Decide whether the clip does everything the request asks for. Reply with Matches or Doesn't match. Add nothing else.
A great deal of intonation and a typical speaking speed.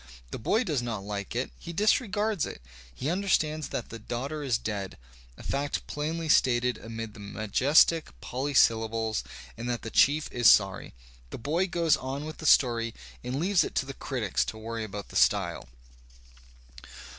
Matches